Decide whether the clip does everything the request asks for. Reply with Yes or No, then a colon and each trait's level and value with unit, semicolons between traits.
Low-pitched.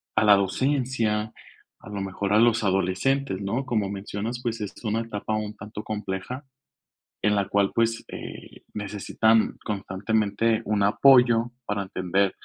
Yes: low, 105 Hz